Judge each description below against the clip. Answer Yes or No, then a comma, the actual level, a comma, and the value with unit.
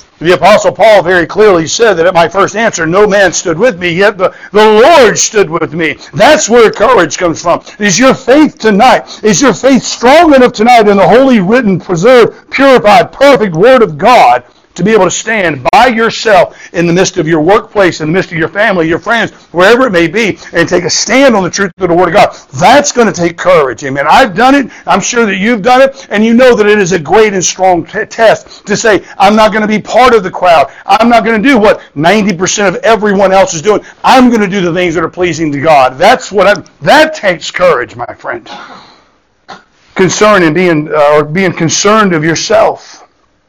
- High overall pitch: Yes, high, 205 Hz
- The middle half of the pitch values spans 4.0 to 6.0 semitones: Yes, average, 5.1 semitones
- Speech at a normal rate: No, fast, 225 wpm